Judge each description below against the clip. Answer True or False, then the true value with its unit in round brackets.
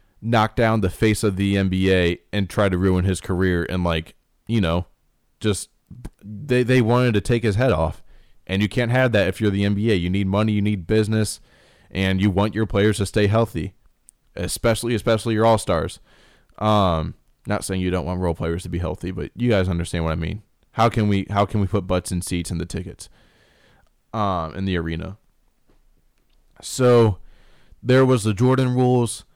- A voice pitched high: False (100 Hz)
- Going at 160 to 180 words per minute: False (190 wpm)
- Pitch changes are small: False (3.4 semitones)